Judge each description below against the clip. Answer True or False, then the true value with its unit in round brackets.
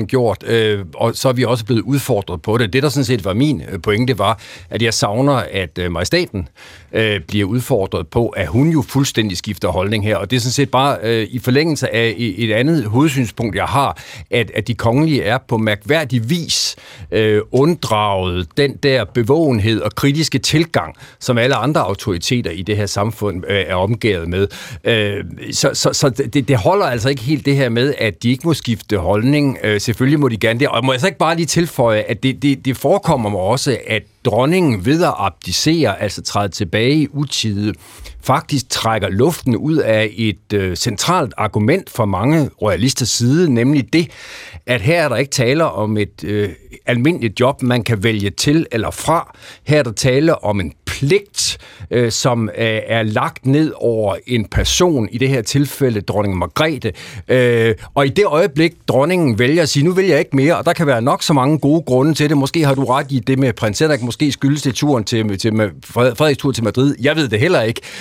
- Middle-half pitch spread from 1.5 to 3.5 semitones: False (4.9 semitones)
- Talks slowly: False (205 wpm)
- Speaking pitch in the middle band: False (125 Hz)